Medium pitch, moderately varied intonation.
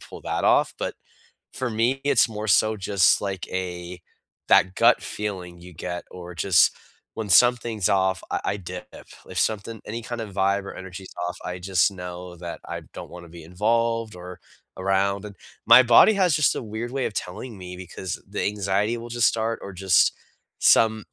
No: low, 100 Hz; average, 3.8 semitones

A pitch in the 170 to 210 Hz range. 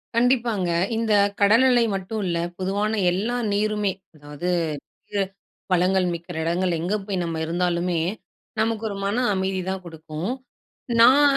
Yes: high, 190 Hz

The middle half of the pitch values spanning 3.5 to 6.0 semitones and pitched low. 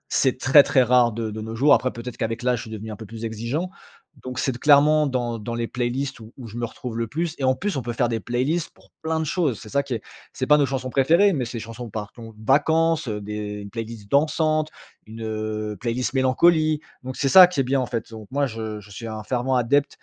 Yes: average, 3.9 semitones; low, 125 Hz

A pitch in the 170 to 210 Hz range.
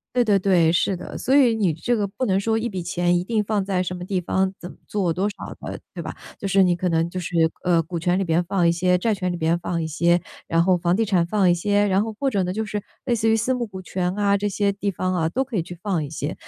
Yes: medium, 185 Hz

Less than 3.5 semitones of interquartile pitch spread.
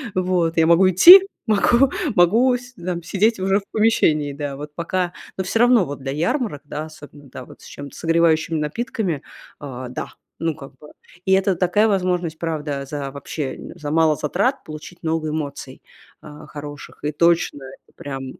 No: average, 4.5 semitones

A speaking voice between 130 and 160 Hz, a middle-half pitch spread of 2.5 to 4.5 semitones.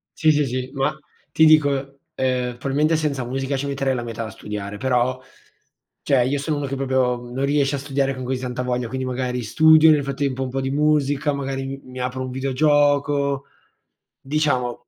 No: low, 135 Hz; narrow, 2.0 semitones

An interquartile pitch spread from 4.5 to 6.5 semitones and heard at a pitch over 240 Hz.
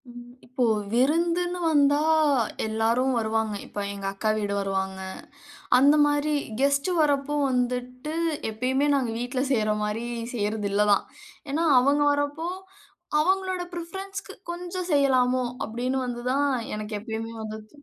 Yes: average, 5.0 semitones; very high, 255 Hz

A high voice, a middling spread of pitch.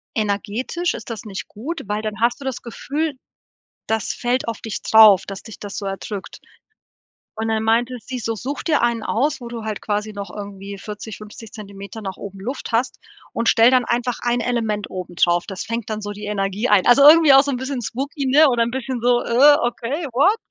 Yes: high, 230 Hz; average, 3.3 semitones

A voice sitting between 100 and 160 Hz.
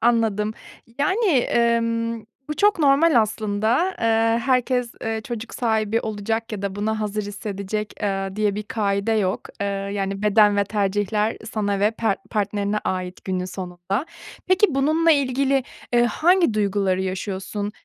No: high, 215 Hz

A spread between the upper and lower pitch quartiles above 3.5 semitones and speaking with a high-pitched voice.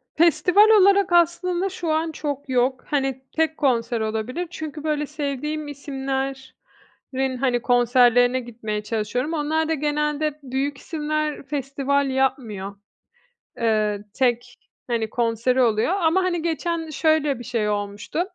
Yes: average, 4.4 semitones; very high, 275 Hz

